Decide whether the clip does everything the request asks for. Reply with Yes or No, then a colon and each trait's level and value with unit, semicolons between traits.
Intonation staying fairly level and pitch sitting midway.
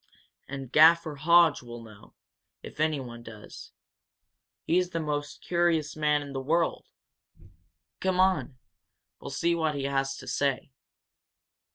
No: average, 3.7 semitones; medium, 150 Hz